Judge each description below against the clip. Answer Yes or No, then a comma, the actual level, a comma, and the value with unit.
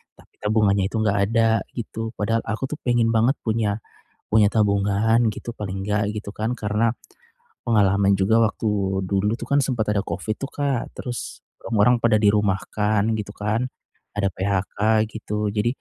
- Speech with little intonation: Yes, narrow, 2.0 semitones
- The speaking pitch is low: Yes, low, 105 Hz